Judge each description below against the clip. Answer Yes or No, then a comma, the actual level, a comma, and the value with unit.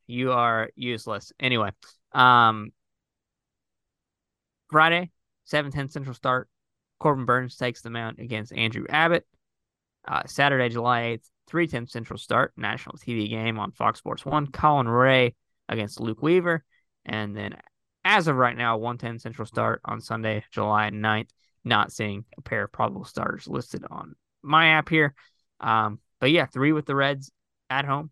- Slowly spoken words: No, average, 155 wpm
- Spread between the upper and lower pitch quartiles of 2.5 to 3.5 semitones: No, average, 4.1 semitones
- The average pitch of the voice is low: Yes, low, 120 Hz